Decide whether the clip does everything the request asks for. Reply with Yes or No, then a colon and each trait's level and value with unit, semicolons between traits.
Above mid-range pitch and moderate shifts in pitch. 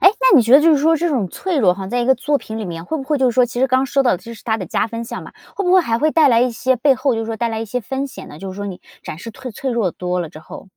Yes: high, 245 Hz; average, 4.0 semitones